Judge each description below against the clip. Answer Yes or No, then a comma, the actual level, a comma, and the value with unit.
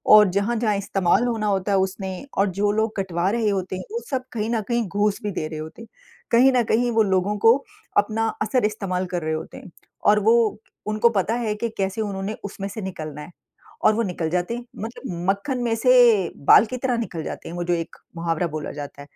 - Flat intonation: No, average, 3.7 semitones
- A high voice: Yes, high, 205 Hz